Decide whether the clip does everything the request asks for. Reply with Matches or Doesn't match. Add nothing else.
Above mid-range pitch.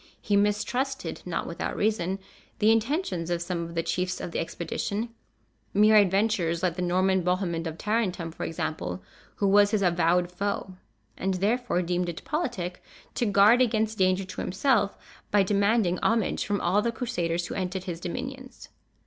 Matches